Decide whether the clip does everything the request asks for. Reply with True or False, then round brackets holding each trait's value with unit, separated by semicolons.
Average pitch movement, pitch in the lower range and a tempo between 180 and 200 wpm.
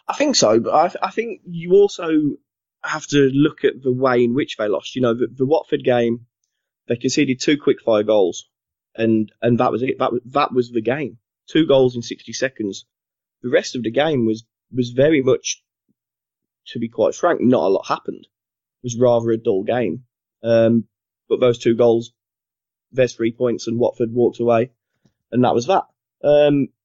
True (3.3 semitones; 120 Hz; 195 wpm)